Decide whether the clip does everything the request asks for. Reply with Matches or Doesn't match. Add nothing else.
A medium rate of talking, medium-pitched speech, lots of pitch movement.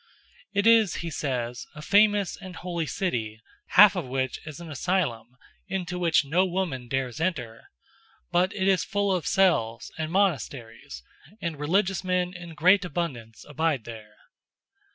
Matches